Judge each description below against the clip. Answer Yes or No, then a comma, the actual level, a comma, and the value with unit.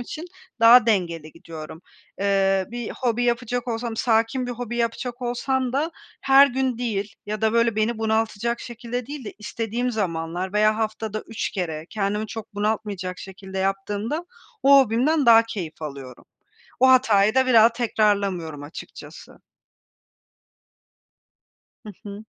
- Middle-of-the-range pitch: No, high, 220 Hz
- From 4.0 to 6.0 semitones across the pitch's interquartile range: No, average, 3.5 semitones